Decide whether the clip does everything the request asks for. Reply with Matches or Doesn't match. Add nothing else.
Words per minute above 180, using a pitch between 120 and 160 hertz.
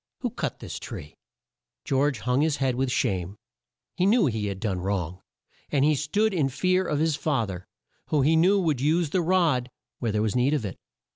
Matches